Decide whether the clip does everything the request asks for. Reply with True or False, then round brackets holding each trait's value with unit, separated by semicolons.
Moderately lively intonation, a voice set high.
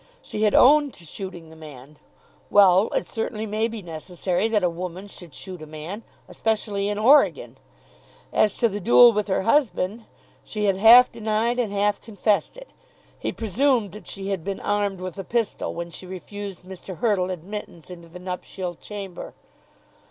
True (3.3 semitones; 200 Hz)